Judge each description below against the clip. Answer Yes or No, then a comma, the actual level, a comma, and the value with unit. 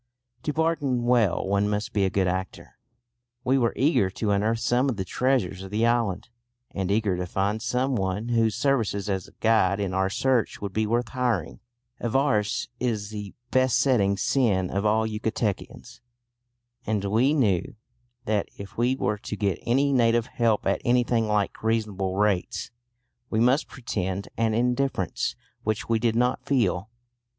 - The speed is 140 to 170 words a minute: Yes, average, 160 wpm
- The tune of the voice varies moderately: Yes, average, 3.6 semitones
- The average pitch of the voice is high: No, low, 110 Hz